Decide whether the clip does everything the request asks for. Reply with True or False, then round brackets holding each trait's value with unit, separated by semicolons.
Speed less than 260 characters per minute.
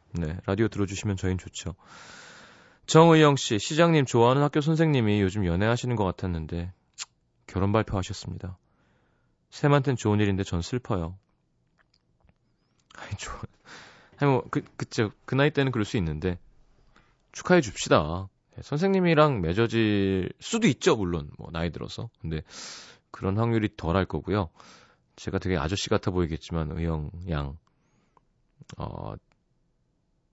False (280 characters per minute)